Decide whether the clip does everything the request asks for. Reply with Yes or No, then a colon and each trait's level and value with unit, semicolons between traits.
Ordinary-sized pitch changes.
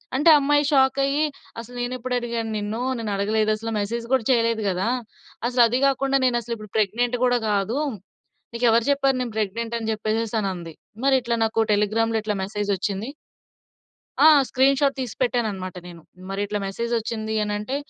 Yes: average, 3.1 semitones